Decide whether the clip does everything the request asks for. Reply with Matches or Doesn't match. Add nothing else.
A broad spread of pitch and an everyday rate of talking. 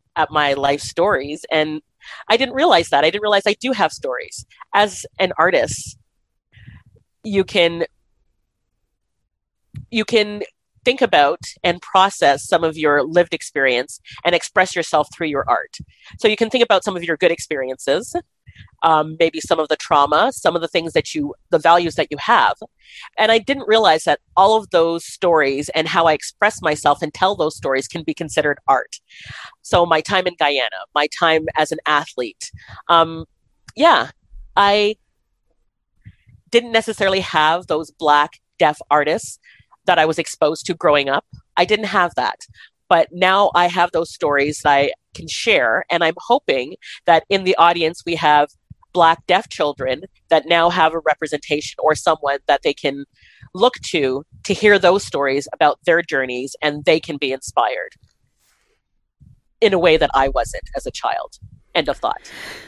Doesn't match